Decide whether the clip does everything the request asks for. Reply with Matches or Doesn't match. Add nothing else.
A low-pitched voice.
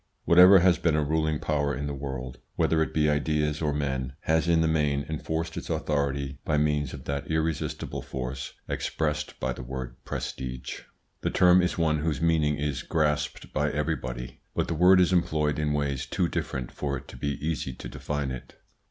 Matches